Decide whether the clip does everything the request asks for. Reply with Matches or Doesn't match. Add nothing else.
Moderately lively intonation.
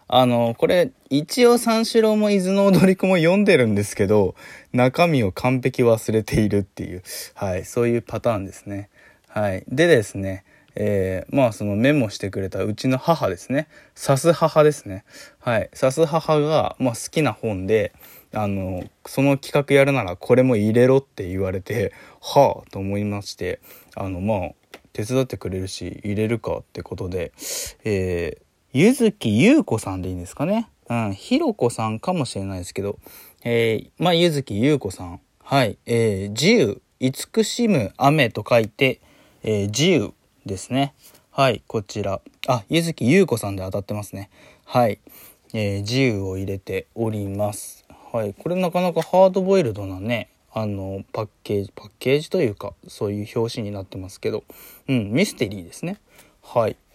Doesn't match